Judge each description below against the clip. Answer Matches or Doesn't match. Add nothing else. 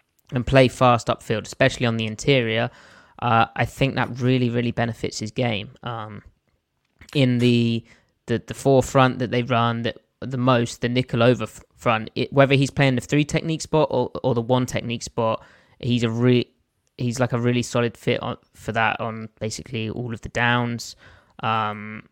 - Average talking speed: Matches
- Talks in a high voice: Doesn't match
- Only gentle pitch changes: Matches